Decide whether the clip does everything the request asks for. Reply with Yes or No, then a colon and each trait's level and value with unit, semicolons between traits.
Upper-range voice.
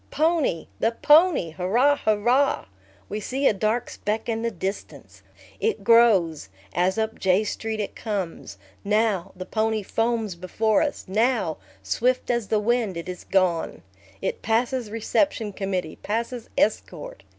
Yes: high, 220 Hz